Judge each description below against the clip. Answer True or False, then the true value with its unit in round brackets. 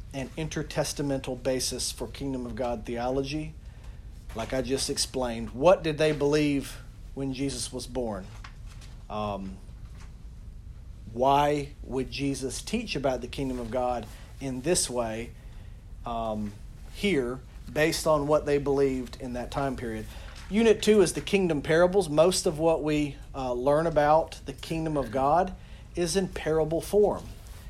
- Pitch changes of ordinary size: True (4.5 semitones)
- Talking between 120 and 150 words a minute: True (140 wpm)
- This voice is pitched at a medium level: False (130 Hz)